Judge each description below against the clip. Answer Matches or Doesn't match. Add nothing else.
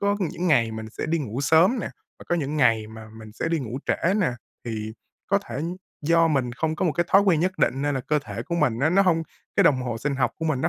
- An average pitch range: Doesn't match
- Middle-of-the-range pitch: Matches